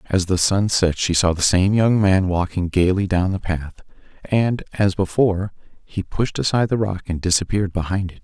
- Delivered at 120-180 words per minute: No, average, 195 wpm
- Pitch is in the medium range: No, very low, 95 Hz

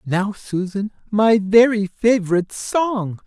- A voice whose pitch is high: Yes, high, 205 Hz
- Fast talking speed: No, slow, 110 wpm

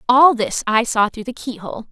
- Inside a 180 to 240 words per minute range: No, fast, 250 wpm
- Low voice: No, high, 230 Hz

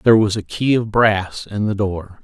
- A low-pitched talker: Yes, low, 105 Hz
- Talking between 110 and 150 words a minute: No, fast, 240 wpm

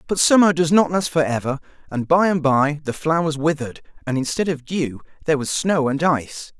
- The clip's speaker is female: No, male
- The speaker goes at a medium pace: No, fast, 210 wpm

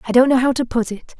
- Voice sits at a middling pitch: No, high, 245 Hz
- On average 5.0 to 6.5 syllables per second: No, 6.9 syllables/s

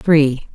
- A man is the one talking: No, female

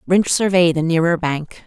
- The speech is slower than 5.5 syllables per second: Yes, 4.6 syllables/s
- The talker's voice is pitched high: No, medium, 170 Hz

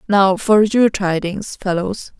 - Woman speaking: Yes, female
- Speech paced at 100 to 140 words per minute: Yes, slow, 135 wpm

